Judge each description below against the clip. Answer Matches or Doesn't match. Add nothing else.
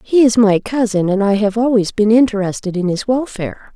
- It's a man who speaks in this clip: Doesn't match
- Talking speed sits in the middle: Doesn't match